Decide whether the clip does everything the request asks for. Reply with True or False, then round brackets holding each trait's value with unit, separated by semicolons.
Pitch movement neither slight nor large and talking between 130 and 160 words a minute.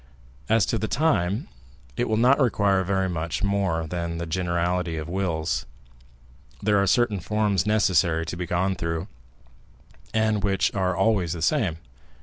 True (3.7 semitones; 150 wpm)